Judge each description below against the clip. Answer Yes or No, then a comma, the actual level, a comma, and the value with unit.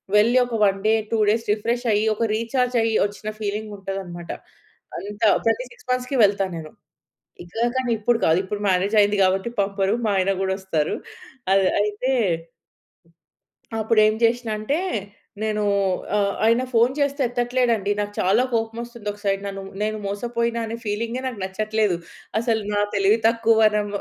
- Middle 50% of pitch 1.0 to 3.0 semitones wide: Yes, average, 2.7 semitones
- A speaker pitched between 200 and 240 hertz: Yes, high, 215 Hz